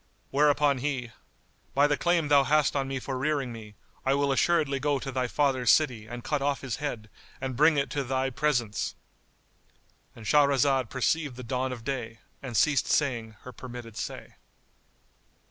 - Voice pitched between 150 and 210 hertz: No, low, 135 Hz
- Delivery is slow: No, average, 165 wpm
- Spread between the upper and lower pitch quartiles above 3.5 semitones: No, average, 2.8 semitones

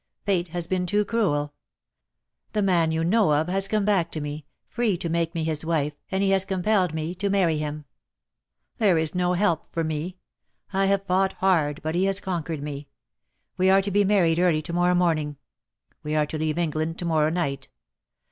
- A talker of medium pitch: Yes, medium, 175 Hz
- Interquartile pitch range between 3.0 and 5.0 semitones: Yes, average, 3.6 semitones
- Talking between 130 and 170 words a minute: No, average, 200 wpm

